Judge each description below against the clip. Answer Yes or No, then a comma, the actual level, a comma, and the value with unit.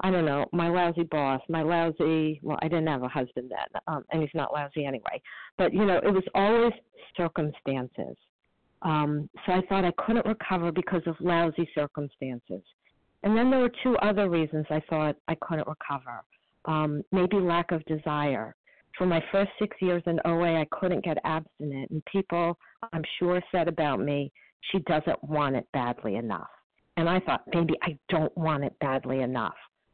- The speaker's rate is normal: Yes, average, 180 wpm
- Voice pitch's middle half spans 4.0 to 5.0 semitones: No, average, 3.3 semitones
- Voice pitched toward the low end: No, medium, 165 Hz